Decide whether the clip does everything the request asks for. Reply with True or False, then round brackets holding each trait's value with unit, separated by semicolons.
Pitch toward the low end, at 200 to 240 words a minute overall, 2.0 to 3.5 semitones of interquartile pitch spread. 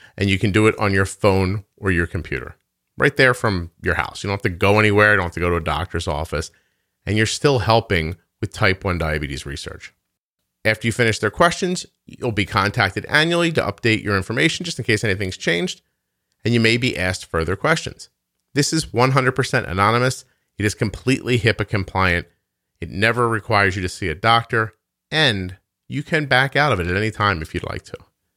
False (105 Hz; 205 wpm; 4.7 semitones)